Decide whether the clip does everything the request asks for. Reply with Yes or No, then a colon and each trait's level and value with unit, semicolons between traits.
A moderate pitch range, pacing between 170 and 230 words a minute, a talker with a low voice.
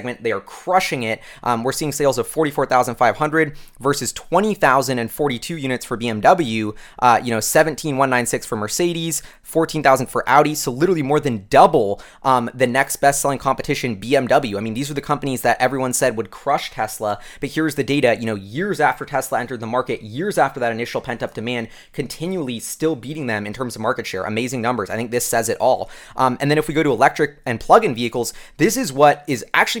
Yes: average, 4.0 semitones; average, 200 wpm; low, 130 Hz